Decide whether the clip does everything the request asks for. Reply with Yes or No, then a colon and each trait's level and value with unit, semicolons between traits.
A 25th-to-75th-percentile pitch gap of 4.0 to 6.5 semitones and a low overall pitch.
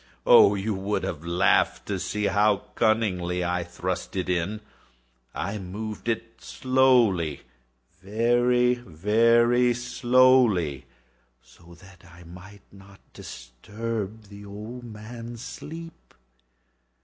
Yes: average, 4.6 semitones; low, 105 Hz